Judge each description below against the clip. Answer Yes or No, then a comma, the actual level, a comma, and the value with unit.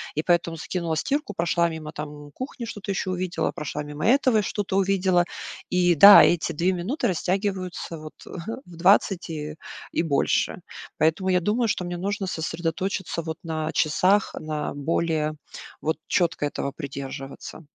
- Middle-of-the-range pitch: Yes, medium, 170 Hz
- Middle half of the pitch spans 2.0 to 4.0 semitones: Yes, average, 3.6 semitones